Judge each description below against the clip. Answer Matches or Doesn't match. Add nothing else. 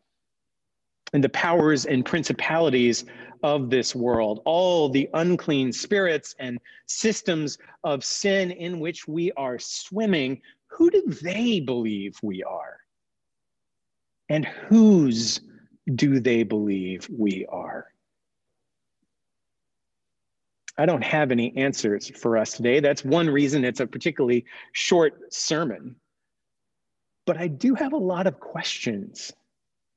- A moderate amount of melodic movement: Doesn't match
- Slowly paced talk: Matches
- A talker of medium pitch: Matches